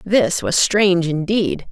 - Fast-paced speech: No, average, 140 wpm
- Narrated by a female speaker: Yes, female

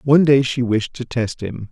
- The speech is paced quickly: Yes, fast, 245 wpm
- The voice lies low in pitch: Yes, low, 125 Hz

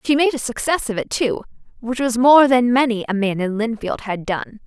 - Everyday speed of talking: No, fast, 230 wpm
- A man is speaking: No, female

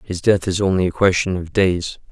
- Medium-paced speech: No, fast, 225 wpm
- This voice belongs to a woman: No, male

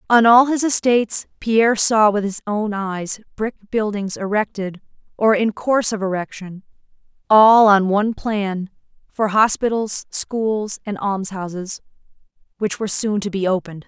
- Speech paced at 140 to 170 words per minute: Yes, average, 145 wpm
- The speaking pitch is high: Yes, high, 210 Hz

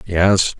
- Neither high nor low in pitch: No, very low, 90 Hz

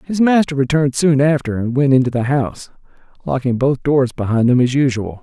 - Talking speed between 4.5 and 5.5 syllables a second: No, 5.7 syllables/s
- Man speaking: Yes, male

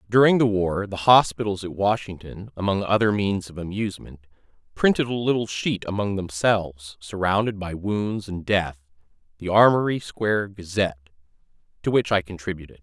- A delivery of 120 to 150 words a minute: Yes, average, 145 wpm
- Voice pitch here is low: Yes, low, 100 Hz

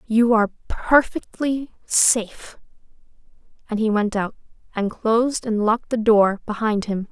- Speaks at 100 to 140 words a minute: Yes, slow, 135 wpm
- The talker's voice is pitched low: No, high, 220 Hz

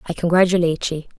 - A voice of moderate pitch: Yes, medium, 170 Hz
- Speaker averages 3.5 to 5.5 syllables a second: No, 6.9 syllables/s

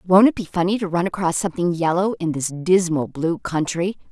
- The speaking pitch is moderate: Yes, medium, 175 Hz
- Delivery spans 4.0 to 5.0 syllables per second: No, 5.5 syllables/s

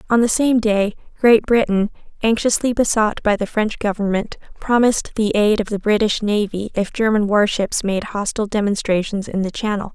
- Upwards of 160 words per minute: Yes, average, 170 wpm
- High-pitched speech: Yes, high, 210 Hz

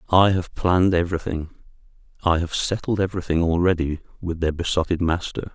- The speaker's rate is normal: No, slow, 130 wpm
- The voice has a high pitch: No, very low, 85 Hz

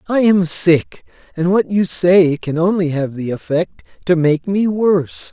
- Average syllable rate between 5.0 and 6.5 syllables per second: No, 4.2 syllables/s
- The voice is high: No, medium, 175 Hz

